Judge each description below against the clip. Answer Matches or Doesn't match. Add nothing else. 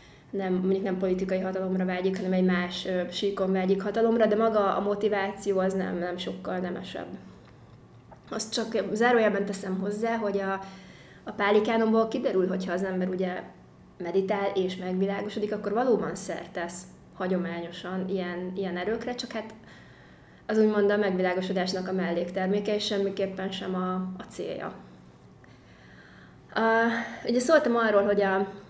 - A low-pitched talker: Doesn't match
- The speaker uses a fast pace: Doesn't match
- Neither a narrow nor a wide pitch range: Doesn't match